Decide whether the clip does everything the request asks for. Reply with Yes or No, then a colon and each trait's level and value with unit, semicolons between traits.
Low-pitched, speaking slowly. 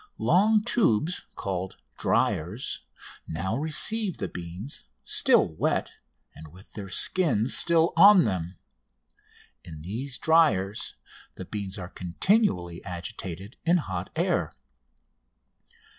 Yes: low, 105 Hz; slow, 105 wpm